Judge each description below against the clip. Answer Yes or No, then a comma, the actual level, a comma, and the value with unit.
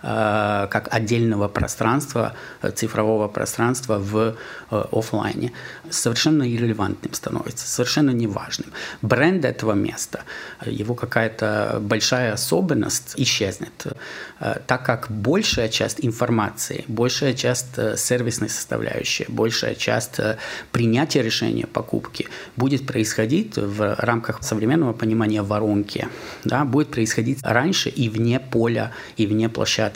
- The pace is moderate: No, slow, 100 wpm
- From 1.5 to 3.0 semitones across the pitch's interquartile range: Yes, narrow, 2.4 semitones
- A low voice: Yes, low, 115 Hz